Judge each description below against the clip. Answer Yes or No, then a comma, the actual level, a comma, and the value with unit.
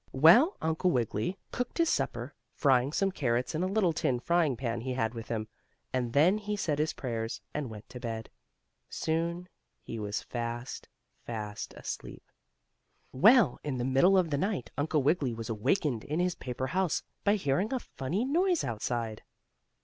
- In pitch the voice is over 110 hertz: Yes, medium, 140 Hz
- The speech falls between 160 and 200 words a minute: Yes, average, 170 wpm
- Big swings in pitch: Yes, wide, 7.4 semitones